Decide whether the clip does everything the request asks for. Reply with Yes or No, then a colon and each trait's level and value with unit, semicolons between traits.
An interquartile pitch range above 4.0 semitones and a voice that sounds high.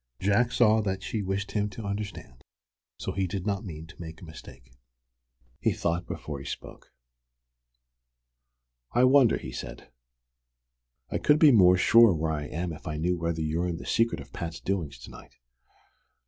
No: average, 4.5 semitones; very low, 90 Hz